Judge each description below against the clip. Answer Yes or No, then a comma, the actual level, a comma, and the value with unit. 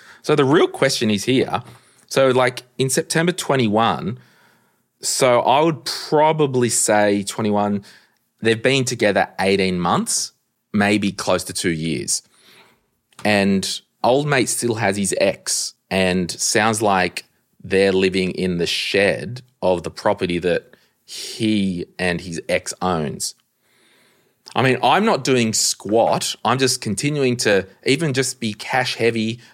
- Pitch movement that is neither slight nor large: Yes, average, 5.0 semitones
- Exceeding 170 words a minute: No, slow, 135 wpm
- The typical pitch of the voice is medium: No, low, 110 Hz